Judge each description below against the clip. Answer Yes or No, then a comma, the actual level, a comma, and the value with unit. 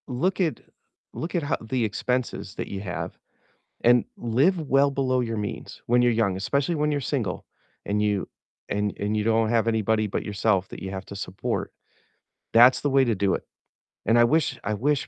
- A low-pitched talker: Yes, low, 115 Hz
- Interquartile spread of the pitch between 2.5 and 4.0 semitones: No, average, 4.6 semitones